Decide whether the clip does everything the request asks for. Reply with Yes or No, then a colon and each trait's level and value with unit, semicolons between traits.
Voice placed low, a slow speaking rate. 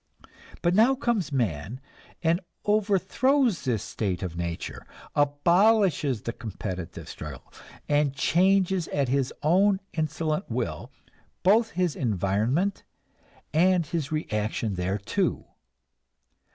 No: medium, 150 Hz; slow, 100 wpm